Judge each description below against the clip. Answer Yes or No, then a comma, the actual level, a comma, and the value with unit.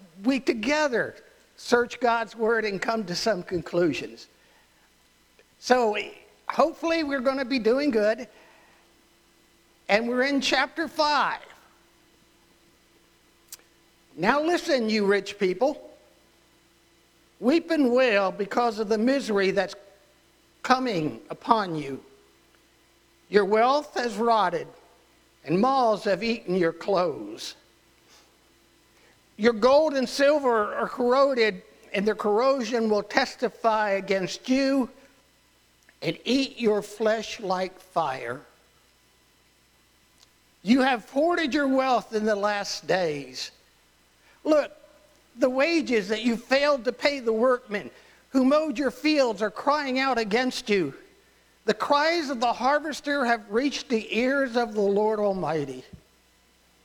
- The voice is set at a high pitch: Yes, high, 230 Hz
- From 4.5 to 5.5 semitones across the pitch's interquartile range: Yes, average, 5.1 semitones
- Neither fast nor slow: No, slow, 115 wpm